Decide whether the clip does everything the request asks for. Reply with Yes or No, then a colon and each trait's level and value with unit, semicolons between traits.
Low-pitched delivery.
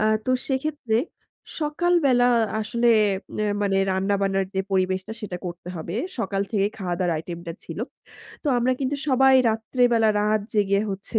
No: high, 210 Hz